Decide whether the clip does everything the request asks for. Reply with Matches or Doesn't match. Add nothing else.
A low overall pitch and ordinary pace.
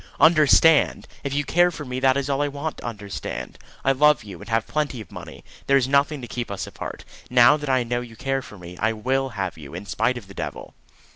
Doesn't match